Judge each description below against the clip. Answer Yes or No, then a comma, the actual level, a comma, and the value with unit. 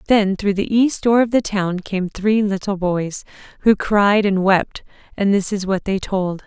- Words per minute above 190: Yes, fast, 205 wpm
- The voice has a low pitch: No, high, 200 Hz